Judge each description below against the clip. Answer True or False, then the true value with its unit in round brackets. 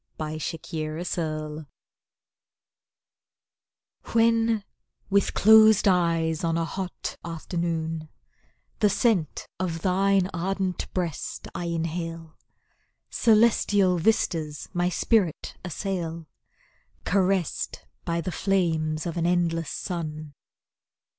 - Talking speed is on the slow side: True (90 wpm)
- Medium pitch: True (170 Hz)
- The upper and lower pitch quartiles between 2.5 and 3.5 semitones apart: True (3.0 semitones)